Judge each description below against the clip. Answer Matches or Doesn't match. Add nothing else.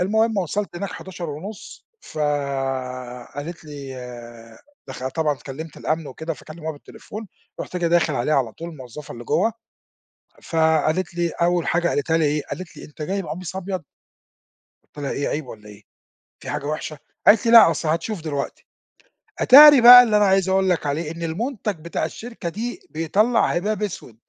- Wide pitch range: Doesn't match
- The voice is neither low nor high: Matches